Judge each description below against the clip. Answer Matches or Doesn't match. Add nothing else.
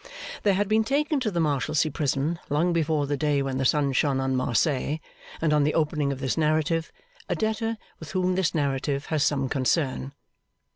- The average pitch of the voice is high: Doesn't match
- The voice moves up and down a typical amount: Matches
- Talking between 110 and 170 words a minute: Doesn't match